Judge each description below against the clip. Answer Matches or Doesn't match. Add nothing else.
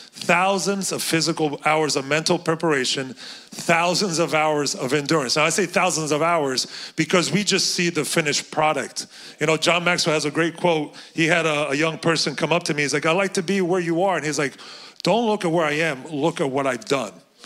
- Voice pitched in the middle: Matches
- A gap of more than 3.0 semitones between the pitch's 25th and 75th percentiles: Doesn't match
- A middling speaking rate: Doesn't match